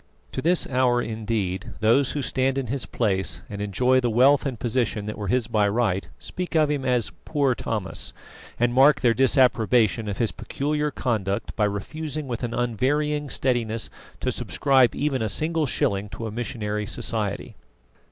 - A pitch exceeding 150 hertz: No, low, 120 Hz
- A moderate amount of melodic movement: Yes, average, 4.1 semitones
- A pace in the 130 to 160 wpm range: No, average, 170 wpm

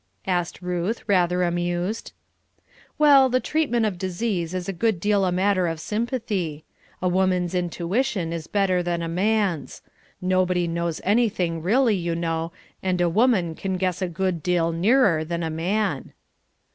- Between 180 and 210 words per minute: No, average, 155 wpm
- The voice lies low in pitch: No, medium, 180 Hz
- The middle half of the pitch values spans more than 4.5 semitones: No, average, 3.3 semitones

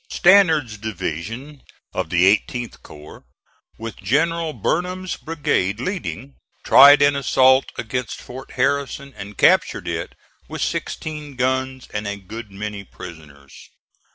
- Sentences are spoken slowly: Yes, slow, 120 wpm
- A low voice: Yes, low, 130 Hz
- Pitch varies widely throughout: Yes, wide, 5.9 semitones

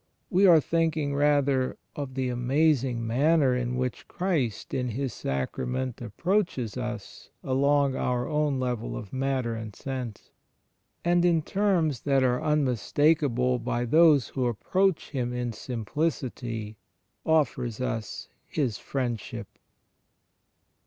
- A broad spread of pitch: No, average, 3.7 semitones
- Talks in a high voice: No, low, 130 Hz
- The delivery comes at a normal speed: No, slow, 120 wpm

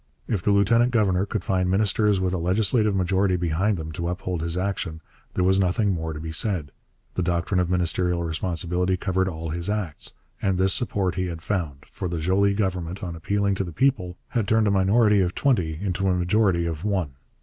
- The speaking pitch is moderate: No, very low, 95 Hz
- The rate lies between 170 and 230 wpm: Yes, fast, 205 wpm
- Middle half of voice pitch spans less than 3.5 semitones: Yes, average, 2.7 semitones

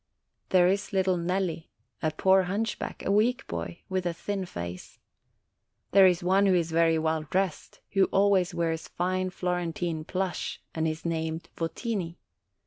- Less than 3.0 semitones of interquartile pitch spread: Yes, narrow, 2.6 semitones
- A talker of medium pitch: Yes, medium, 180 Hz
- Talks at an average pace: Yes, average, 155 wpm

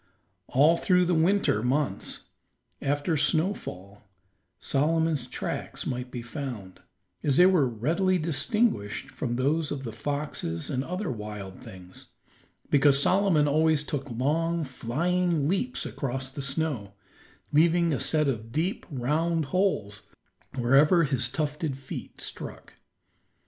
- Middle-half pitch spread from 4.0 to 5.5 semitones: Yes, average, 4.8 semitones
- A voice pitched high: No, medium, 145 Hz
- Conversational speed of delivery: No, slow, 125 wpm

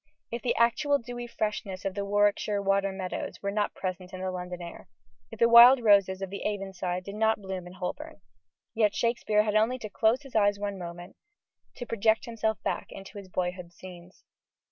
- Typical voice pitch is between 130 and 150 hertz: No, high, 205 Hz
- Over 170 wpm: Yes, average, 195 wpm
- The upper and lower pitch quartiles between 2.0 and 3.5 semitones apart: Yes, average, 3.2 semitones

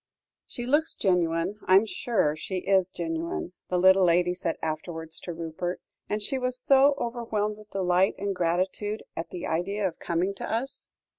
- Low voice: No, medium, 185 Hz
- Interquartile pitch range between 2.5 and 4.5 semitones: Yes, average, 3.7 semitones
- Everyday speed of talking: Yes, average, 170 wpm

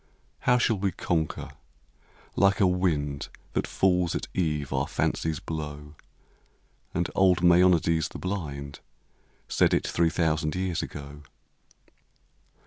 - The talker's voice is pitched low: Yes, very low, 85 Hz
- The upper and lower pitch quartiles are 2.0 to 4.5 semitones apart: Yes, average, 3.7 semitones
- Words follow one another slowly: Yes, slow, 130 wpm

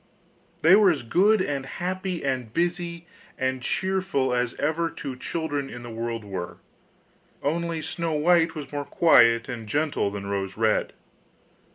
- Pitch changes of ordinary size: No, wide, 6.1 semitones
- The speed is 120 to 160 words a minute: Yes, average, 150 wpm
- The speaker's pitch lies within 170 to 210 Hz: No, medium, 145 Hz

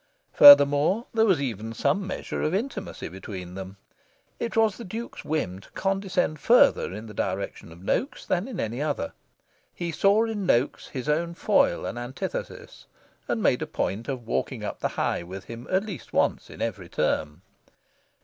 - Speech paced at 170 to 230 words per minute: Yes, average, 175 wpm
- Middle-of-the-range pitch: Yes, medium, 145 Hz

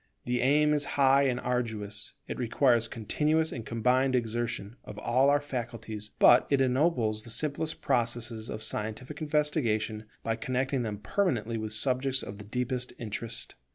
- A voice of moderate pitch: No, low, 120 Hz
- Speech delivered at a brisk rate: No, average, 155 wpm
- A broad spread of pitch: No, average, 3.4 semitones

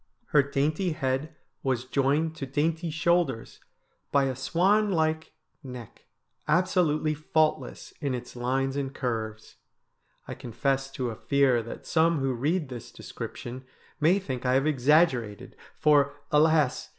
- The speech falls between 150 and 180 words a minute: No, slow, 135 wpm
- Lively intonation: No, average, 3.6 semitones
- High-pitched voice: No, medium, 140 Hz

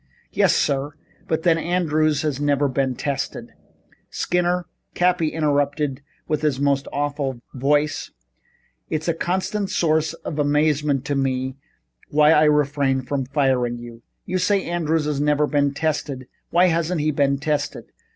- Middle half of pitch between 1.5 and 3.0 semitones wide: Yes, narrow, 2.4 semitones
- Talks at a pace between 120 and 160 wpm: Yes, average, 145 wpm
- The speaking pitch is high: No, medium, 150 Hz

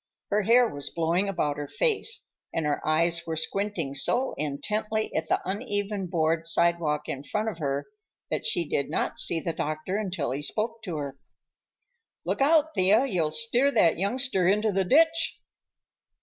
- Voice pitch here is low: No, medium, 185 Hz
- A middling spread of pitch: No, wide, 5.7 semitones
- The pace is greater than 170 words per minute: No, average, 165 wpm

